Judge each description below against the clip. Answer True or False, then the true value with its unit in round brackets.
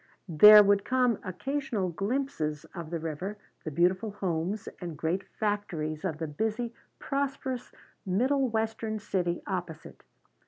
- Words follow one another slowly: True (125 wpm)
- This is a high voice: True (195 Hz)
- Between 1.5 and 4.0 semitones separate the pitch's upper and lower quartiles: False (4.9 semitones)